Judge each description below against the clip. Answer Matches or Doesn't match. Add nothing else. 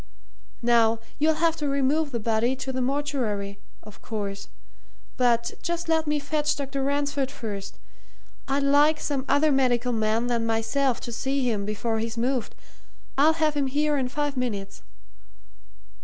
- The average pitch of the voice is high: Matches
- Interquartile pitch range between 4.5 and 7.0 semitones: Doesn't match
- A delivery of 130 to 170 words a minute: Matches